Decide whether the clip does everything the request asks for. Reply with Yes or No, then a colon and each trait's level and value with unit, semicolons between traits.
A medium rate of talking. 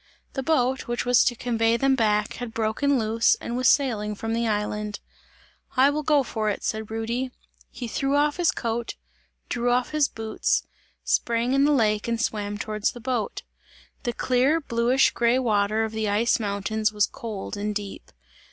Yes: average, 180 wpm